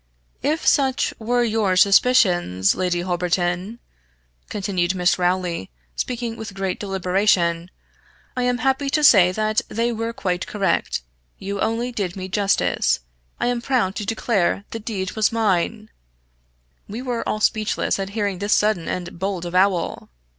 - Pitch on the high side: Yes, high, 200 Hz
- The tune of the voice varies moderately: Yes, average, 4.0 semitones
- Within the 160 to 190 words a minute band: No, average, 145 wpm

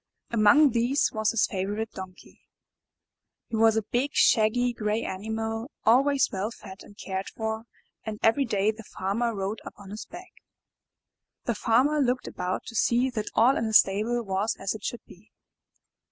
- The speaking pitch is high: Yes, high, 220 Hz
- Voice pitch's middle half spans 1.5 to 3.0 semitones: Yes, average, 2.7 semitones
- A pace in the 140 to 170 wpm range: Yes, average, 165 wpm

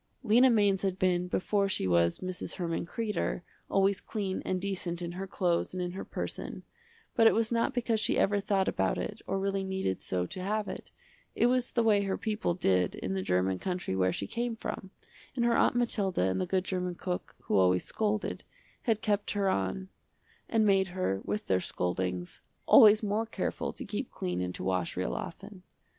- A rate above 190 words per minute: Yes, average, 200 wpm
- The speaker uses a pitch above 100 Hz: Yes, high, 190 Hz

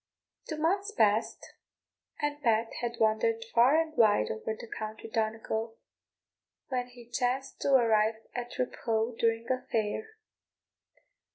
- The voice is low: No, high, 235 Hz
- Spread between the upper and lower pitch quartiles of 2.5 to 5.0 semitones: Yes, average, 3.5 semitones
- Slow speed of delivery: Yes, slow, 125 wpm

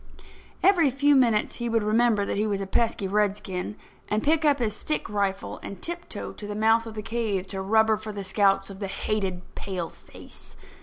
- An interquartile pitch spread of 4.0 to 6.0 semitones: No, average, 2.8 semitones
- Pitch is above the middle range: Yes, high, 210 Hz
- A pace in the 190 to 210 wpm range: Yes, average, 195 wpm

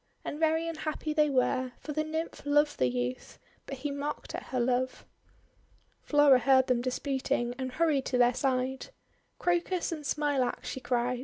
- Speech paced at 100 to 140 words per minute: No, average, 165 wpm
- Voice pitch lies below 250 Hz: No, very high, 270 Hz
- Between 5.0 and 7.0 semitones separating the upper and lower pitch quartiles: No, average, 3.1 semitones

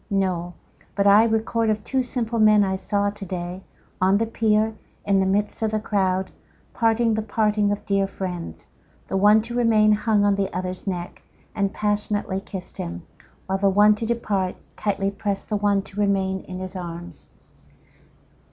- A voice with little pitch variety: Yes, narrow, 2.1 semitones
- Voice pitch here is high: Yes, high, 205 Hz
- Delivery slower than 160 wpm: No, average, 165 wpm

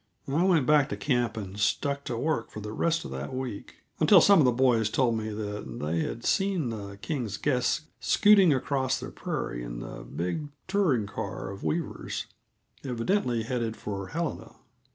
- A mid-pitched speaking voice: No, low, 120 Hz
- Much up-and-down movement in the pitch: Yes, wide, 6.2 semitones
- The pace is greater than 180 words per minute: No, average, 175 wpm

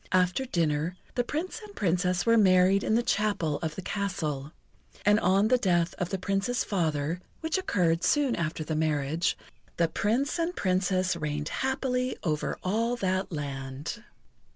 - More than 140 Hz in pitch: Yes, medium, 185 Hz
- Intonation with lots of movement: Yes, wide, 5.7 semitones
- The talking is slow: No, average, 155 wpm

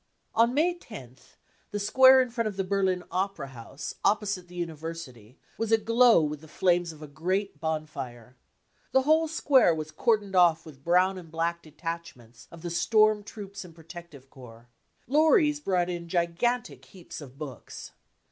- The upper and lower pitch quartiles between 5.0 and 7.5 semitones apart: Yes, wide, 5.5 semitones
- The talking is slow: No, average, 165 wpm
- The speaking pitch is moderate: Yes, medium, 175 Hz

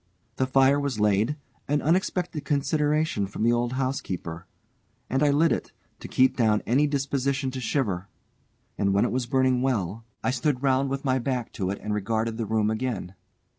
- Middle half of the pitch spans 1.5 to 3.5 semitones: No, average, 4.1 semitones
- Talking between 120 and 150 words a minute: No, average, 180 wpm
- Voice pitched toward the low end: Yes, low, 130 Hz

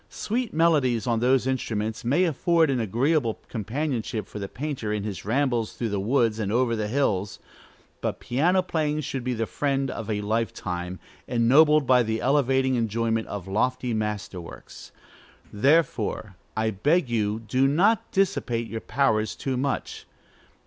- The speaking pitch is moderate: No, low, 120 Hz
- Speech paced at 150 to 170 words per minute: Yes, average, 155 wpm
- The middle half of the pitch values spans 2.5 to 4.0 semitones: No, average, 4.4 semitones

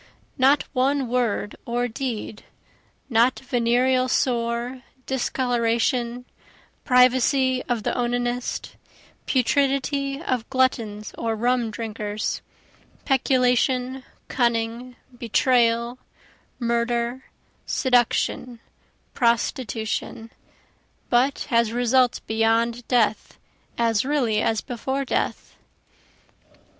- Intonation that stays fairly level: Yes, narrow, 1.9 semitones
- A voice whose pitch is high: Yes, high, 245 Hz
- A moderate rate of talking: No, slow, 80 wpm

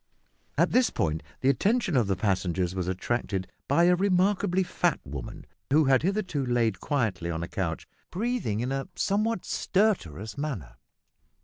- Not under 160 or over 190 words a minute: No, average, 150 wpm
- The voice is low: Yes, low, 130 Hz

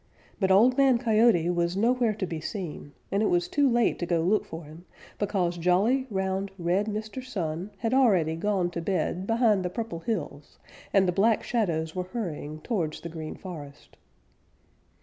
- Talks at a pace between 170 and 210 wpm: Yes, average, 175 wpm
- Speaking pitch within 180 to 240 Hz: Yes, high, 190 Hz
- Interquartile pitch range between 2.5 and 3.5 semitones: No, average, 4.6 semitones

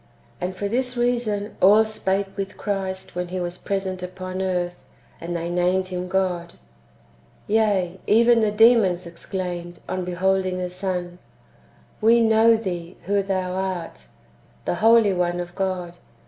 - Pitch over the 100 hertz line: Yes, high, 190 Hz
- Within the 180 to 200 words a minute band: No, average, 145 wpm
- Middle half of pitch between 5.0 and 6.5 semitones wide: No, narrow, 2.4 semitones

